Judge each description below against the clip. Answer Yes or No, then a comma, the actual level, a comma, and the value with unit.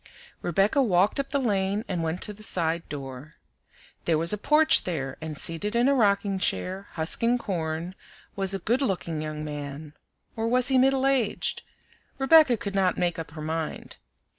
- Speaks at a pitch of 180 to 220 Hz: Yes, high, 190 Hz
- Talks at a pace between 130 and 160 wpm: No, average, 175 wpm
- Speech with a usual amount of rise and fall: No, wide, 6.6 semitones